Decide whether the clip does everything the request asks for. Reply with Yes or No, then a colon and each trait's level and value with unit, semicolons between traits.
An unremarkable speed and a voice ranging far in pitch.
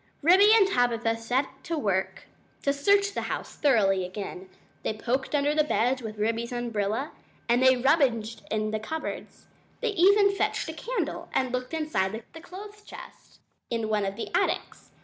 Yes: average, 165 wpm; wide, 6.7 semitones